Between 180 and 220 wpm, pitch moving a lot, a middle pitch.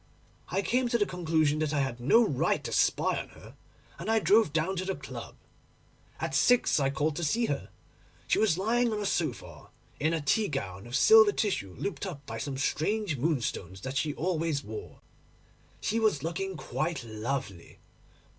Yes: average, 185 wpm; wide, 7.0 semitones; medium, 160 Hz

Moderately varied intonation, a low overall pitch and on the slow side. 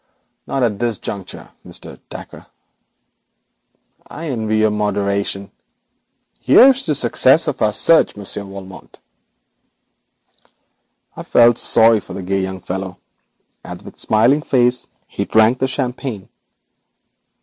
Yes: average, 4.3 semitones; low, 110 Hz; slow, 120 wpm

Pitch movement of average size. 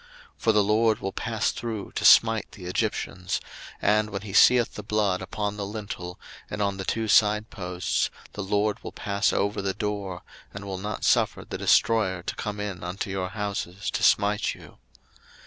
No: narrow, 1.9 semitones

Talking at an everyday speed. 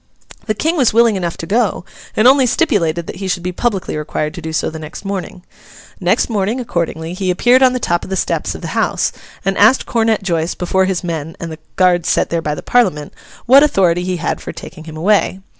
No: fast, 225 wpm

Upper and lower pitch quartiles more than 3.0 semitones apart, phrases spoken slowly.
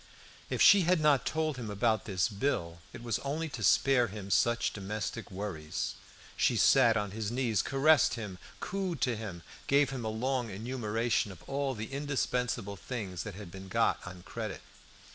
No: average, 5.0 semitones; average, 175 wpm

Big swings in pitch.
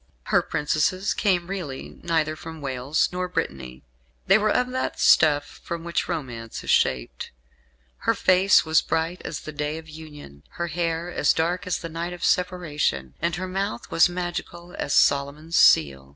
No: average, 3.4 semitones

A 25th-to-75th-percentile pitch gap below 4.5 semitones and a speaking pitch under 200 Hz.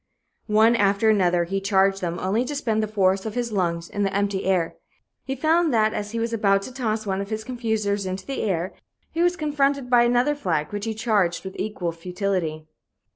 No: average, 3.6 semitones; high, 205 Hz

